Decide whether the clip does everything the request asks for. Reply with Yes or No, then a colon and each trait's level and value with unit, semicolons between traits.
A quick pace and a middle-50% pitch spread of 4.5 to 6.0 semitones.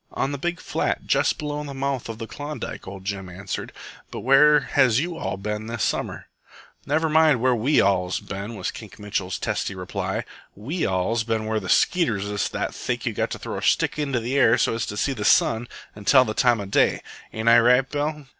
Yes: fast, 220 wpm; wide, 5.5 semitones